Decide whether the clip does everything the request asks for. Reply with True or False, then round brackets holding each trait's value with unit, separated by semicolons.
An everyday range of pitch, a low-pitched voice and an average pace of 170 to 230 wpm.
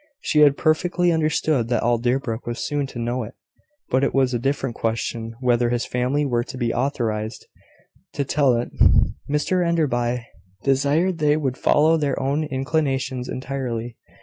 False (3.6 semitones; 130 Hz; 160 wpm)